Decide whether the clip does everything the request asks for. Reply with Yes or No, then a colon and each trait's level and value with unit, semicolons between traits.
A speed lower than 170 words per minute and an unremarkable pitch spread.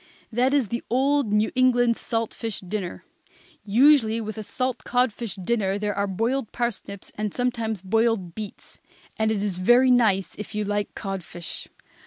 Yes: average, 160 wpm; average, 3.2 semitones